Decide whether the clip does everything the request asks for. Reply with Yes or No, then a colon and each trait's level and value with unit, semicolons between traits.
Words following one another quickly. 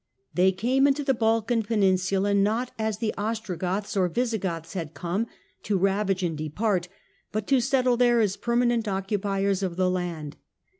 No: average, 160 wpm